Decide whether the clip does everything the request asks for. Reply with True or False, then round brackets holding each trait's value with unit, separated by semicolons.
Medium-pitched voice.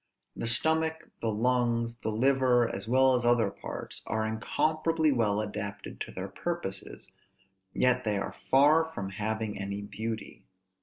False (115 Hz)